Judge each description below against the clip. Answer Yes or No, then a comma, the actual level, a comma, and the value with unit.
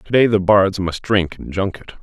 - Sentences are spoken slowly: No, fast, 205 wpm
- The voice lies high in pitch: No, very low, 95 Hz